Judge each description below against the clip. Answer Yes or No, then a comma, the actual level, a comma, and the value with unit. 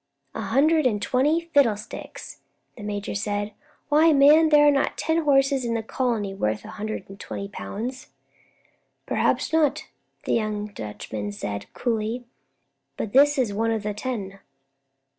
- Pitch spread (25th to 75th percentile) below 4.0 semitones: No, wide, 5.6 semitones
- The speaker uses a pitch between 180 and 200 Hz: No, high, 230 Hz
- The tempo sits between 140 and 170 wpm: Yes, average, 150 wpm